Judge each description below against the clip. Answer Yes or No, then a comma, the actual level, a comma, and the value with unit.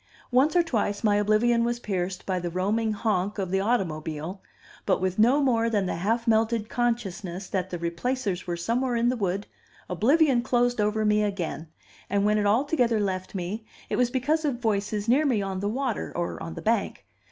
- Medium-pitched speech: No, high, 210 Hz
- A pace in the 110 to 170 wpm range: No, average, 195 wpm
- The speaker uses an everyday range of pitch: Yes, average, 4.1 semitones